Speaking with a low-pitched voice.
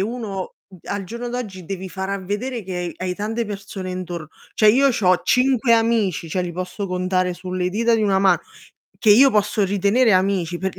No: high, 195 Hz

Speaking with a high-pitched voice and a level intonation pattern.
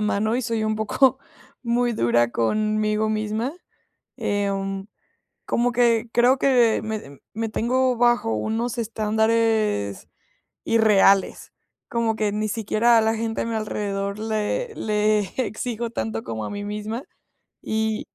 Yes: high, 220 Hz; narrow, 1.9 semitones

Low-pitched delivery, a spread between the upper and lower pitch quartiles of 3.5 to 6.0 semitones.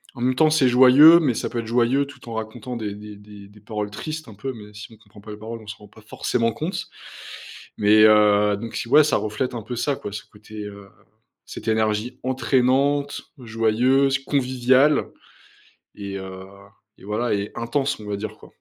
Yes: low, 115 Hz; average, 3.8 semitones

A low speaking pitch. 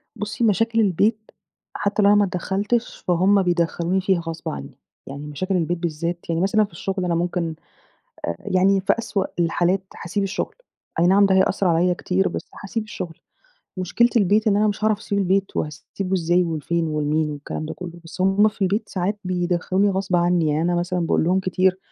No: medium, 185 Hz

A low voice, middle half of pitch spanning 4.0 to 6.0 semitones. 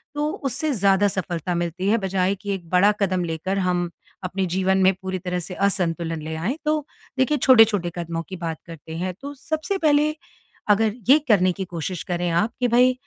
No: high, 190 Hz; average, 4.3 semitones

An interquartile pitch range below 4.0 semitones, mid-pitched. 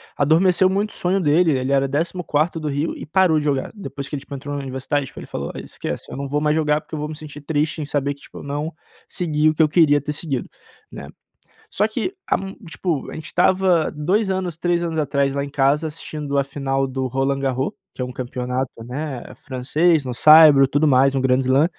Yes: average, 2.9 semitones; medium, 145 Hz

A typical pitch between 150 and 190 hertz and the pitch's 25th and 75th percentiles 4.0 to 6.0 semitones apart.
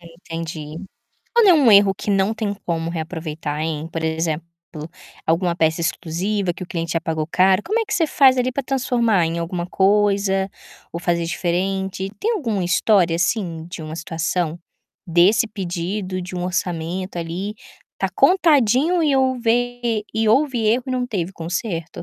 Yes: medium, 185 Hz; average, 5.1 semitones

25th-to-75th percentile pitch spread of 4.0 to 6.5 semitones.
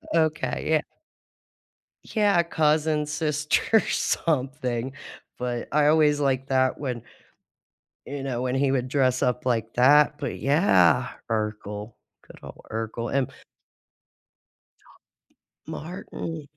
No: average, 3.6 semitones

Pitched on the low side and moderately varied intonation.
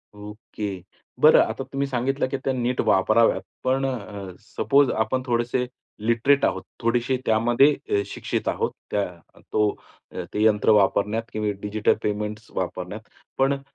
Yes: low, 115 Hz; average, 3.6 semitones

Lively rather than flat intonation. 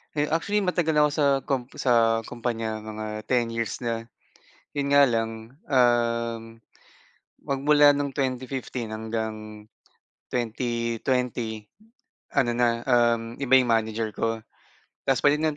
No: average, 3.2 semitones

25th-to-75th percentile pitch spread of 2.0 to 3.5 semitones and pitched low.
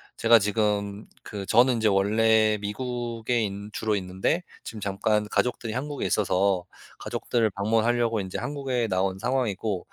Yes: average, 3.0 semitones; low, 110 Hz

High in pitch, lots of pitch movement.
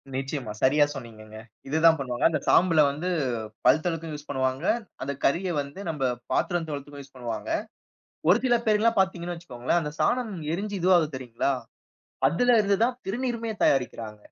No: medium, 155 Hz; wide, 6.1 semitones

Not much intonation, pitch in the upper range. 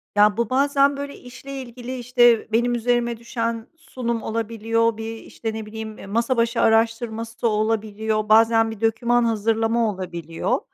Yes: narrow, 1.5 semitones; high, 230 Hz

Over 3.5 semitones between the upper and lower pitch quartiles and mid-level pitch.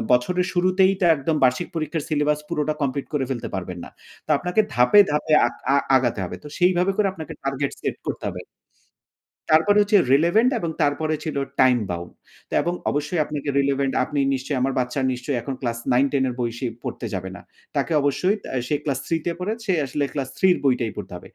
Yes: average, 4.8 semitones; medium, 145 Hz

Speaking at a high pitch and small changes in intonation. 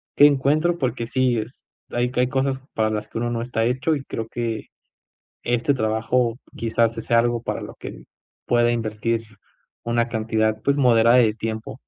No: low, 120 Hz; narrow, 2.0 semitones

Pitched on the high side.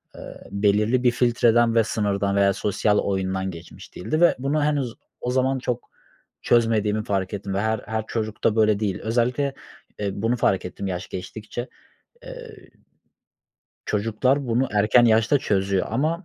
No: low, 110 Hz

